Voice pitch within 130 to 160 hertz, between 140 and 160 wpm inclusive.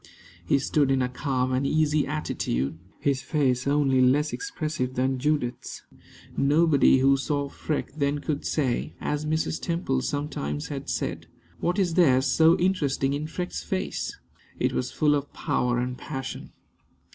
Yes: medium, 140 Hz; average, 150 wpm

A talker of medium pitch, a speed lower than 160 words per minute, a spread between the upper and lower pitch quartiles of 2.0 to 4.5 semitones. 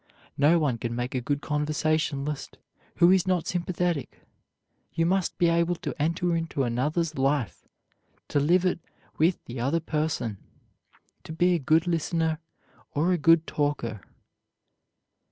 Yes: medium, 155 Hz; average, 140 wpm; average, 3.2 semitones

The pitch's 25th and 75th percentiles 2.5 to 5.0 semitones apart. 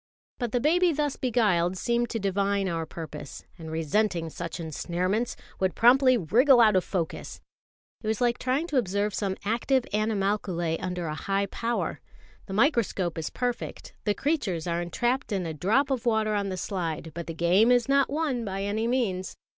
No: wide, 5.4 semitones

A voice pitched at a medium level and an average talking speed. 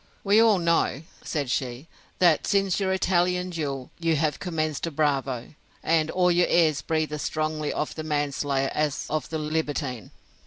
Yes: medium, 155 Hz; average, 165 wpm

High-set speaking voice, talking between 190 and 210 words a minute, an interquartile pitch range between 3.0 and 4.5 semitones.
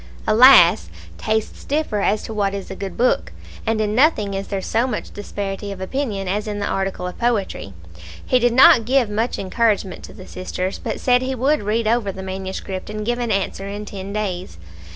Yes: high, 210 Hz; average, 200 wpm; average, 3.4 semitones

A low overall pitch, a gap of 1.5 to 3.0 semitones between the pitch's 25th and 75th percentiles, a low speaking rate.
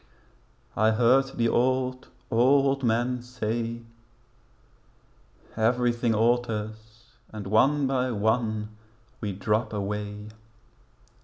Yes: low, 115 Hz; narrow, 2.5 semitones; slow, 85 wpm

